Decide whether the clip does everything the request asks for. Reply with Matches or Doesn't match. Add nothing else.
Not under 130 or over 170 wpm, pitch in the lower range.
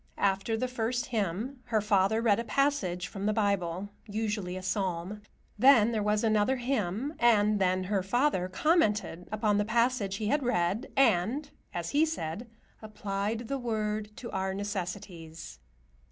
Doesn't match